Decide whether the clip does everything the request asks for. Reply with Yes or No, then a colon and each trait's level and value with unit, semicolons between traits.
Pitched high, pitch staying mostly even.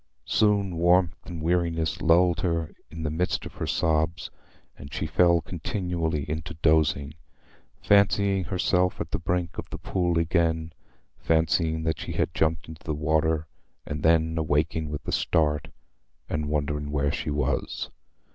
No: very low, 80 Hz; narrow, 2.0 semitones